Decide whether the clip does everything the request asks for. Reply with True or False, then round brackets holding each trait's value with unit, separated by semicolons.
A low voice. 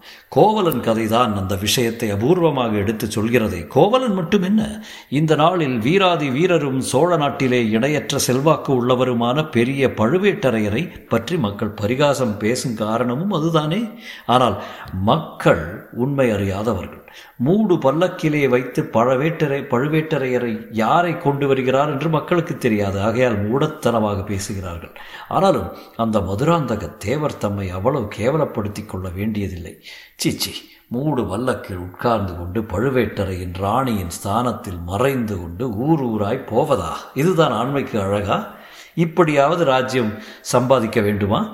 True (125 Hz)